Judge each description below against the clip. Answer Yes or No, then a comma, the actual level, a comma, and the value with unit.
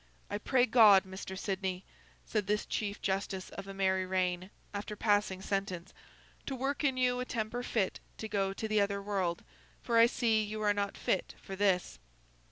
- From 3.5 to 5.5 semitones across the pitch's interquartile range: No, narrow, 2.4 semitones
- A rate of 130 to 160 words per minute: No, average, 180 wpm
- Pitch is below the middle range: No, high, 200 Hz